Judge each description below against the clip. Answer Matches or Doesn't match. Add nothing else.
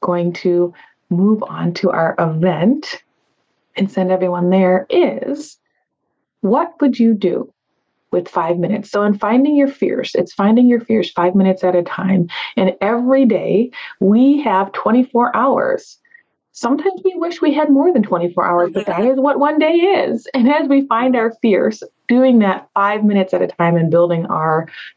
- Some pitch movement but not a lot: Doesn't match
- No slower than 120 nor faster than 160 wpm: Doesn't match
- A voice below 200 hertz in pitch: Doesn't match